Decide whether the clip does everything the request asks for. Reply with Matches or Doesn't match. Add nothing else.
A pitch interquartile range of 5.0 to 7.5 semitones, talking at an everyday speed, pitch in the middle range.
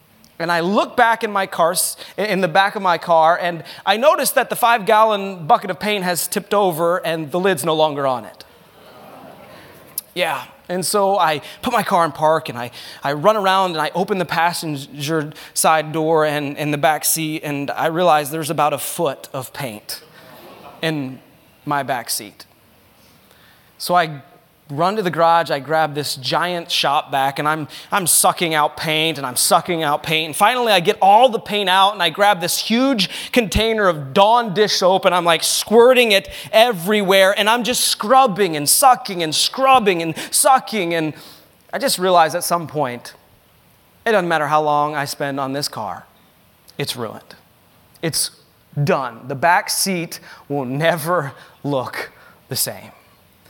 Doesn't match